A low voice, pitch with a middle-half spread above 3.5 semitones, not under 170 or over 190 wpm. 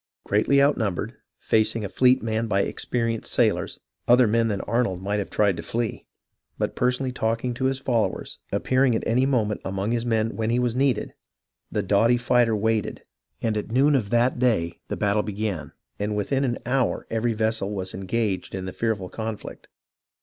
No: low, 115 Hz; average, 2.9 semitones; average, 180 wpm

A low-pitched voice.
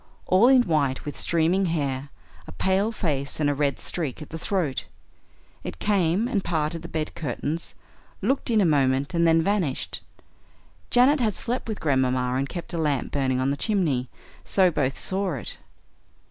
No: medium, 160 Hz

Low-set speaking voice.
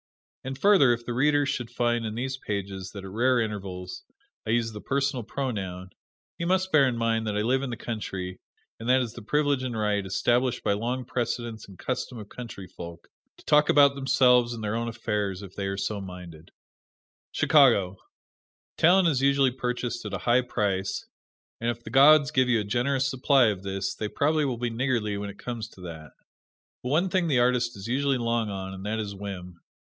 Yes: low, 120 Hz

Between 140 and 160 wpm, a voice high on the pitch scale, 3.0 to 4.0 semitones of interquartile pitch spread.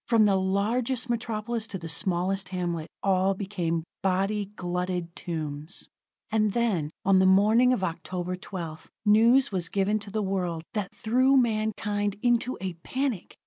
Yes: average, 145 wpm; high, 195 Hz; average, 3.4 semitones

